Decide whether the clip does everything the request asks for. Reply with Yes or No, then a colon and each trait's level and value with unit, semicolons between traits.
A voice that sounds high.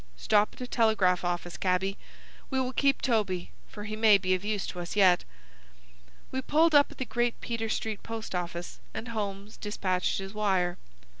Yes: high, 210 Hz